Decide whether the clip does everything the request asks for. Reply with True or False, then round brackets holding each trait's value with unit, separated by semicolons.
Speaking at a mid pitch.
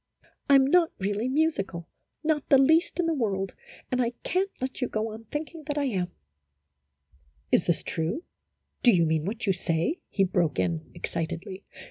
False (215 Hz)